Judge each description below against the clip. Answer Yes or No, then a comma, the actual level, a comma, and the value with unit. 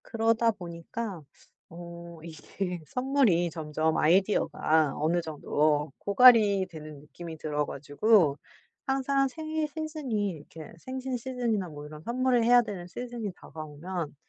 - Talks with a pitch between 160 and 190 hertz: Yes, medium, 185 Hz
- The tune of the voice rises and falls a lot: Yes, wide, 7.4 semitones